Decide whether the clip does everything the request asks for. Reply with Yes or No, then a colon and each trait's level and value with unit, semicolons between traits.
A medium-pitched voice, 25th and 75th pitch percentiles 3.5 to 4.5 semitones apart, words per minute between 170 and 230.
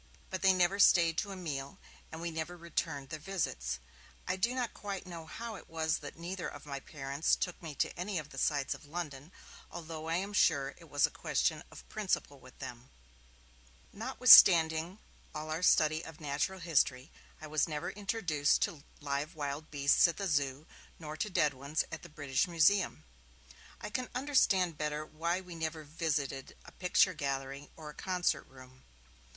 Yes: medium, 160 Hz; average, 3.9 semitones; average, 180 wpm